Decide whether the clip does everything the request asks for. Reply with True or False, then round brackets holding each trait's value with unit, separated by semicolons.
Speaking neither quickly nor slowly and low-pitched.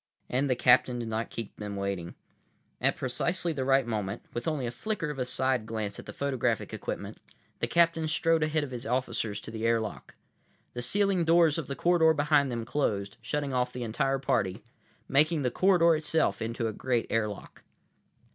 True (185 wpm; 130 Hz)